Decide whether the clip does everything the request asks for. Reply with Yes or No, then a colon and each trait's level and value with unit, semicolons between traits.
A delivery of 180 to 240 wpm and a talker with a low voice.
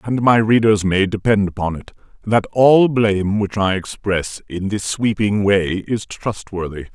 No: average, 165 wpm; low, 100 Hz